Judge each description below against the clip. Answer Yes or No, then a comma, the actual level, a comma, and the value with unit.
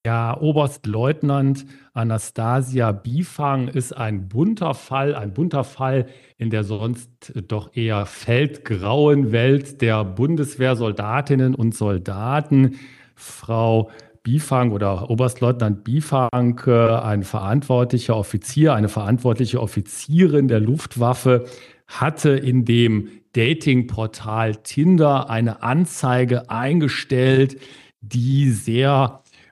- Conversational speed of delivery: No, slow, 95 wpm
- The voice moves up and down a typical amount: Yes, average, 3.4 semitones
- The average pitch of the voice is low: Yes, low, 125 Hz